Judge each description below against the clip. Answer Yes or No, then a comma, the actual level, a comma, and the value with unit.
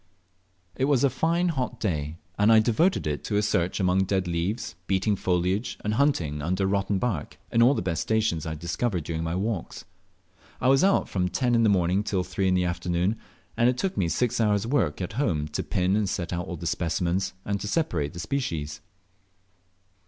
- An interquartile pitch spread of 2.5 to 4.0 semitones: No, average, 5.1 semitones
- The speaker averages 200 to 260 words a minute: Yes, fast, 205 wpm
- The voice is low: Yes, very low, 95 Hz